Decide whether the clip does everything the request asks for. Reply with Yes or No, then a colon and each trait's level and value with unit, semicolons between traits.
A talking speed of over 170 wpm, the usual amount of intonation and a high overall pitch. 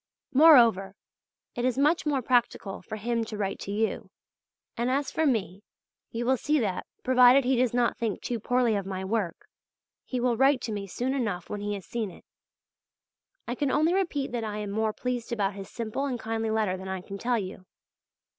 Yes: average, 200 wpm; average, 3.9 semitones; high, 230 Hz